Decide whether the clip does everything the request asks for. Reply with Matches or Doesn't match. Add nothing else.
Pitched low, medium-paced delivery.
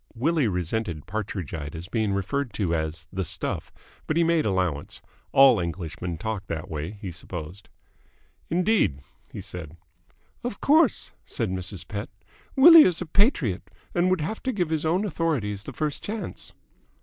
Matches